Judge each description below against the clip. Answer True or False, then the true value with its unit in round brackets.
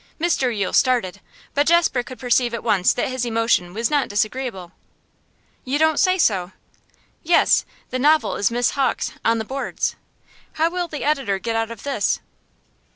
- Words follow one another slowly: False (165 wpm)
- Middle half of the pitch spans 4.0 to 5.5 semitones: True (4.7 semitones)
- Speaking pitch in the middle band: False (245 Hz)